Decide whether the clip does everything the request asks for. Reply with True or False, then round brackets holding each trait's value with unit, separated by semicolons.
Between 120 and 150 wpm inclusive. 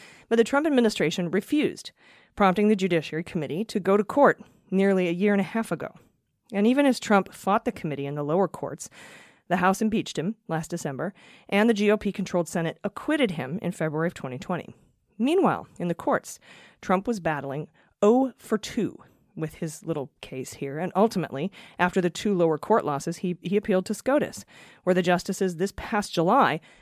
False (185 wpm)